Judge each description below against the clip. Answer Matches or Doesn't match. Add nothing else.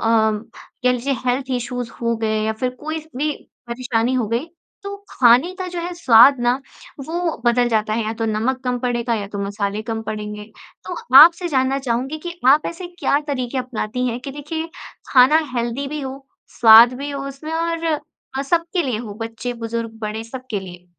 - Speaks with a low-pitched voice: Doesn't match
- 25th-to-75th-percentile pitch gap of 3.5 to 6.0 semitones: Matches